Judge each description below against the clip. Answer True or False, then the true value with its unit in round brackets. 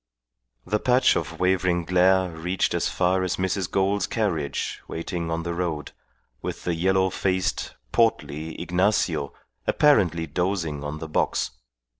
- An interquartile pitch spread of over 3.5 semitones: False (2.5 semitones)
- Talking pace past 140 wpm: False (135 wpm)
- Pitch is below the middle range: True (90 Hz)